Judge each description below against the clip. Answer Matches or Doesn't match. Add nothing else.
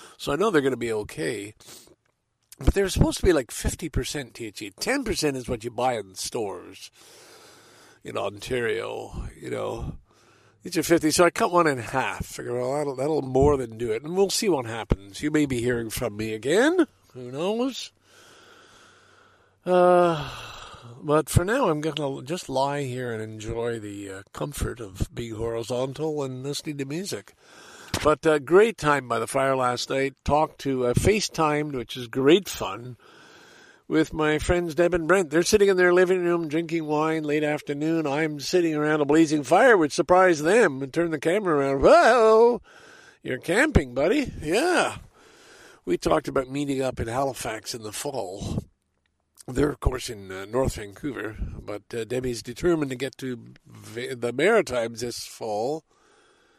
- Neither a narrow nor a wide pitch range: Doesn't match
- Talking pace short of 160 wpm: Doesn't match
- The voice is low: Doesn't match